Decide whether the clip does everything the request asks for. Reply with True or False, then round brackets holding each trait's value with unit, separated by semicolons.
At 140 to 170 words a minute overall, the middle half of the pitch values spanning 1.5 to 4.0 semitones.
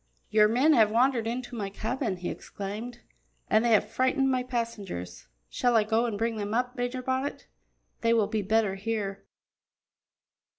True (165 wpm; 2.8 semitones)